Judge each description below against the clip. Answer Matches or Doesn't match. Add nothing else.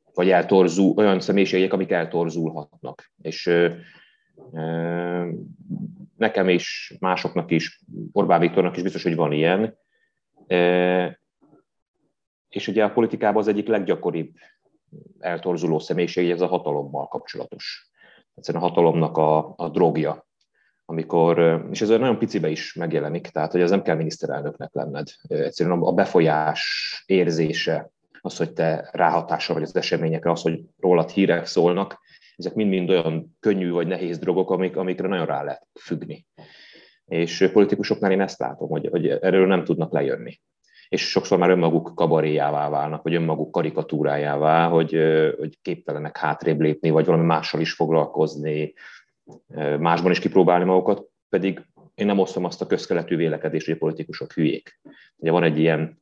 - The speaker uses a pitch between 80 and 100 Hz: Matches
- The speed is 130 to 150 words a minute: Matches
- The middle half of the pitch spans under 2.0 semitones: Doesn't match